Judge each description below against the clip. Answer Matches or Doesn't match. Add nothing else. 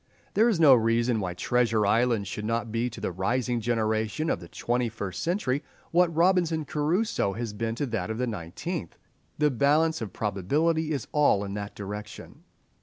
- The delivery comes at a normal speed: Matches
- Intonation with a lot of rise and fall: Matches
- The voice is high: Doesn't match